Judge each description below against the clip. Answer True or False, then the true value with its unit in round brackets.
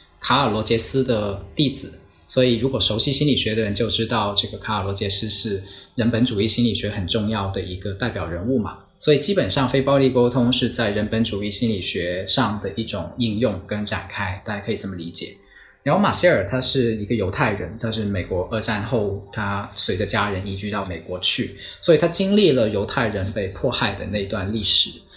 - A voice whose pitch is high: False (110 Hz)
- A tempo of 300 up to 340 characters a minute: True (310 characters per minute)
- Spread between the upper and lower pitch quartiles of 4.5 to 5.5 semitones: False (3.3 semitones)